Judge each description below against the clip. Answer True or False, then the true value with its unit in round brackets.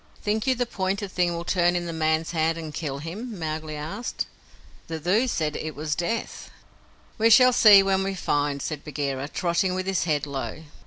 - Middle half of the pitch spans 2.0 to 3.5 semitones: False (4.0 semitones)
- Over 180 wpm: True (195 wpm)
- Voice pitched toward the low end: False (170 Hz)